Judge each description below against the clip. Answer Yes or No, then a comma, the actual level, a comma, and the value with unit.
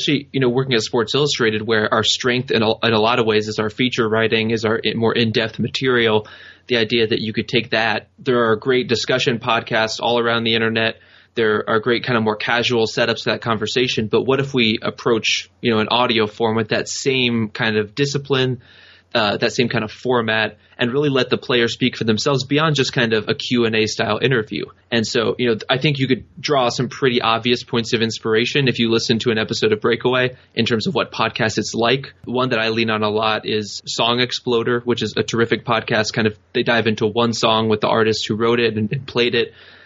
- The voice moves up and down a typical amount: No, narrow, 2.0 semitones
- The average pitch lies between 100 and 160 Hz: Yes, low, 115 Hz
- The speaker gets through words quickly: Yes, fast, 230 wpm